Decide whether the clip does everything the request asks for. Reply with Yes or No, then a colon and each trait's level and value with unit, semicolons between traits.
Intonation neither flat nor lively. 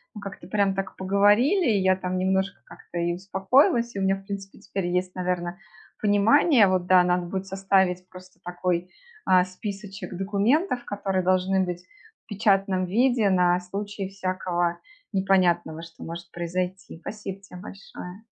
No: narrow, 1.8 semitones